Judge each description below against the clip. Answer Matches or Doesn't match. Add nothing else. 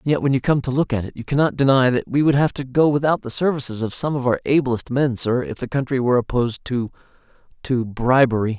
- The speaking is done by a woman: Doesn't match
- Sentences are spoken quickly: Matches